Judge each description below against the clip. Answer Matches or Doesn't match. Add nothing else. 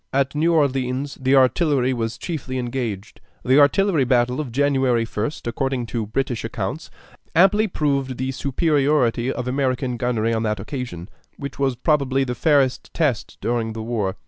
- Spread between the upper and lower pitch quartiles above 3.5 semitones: Doesn't match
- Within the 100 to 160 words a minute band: Matches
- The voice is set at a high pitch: Doesn't match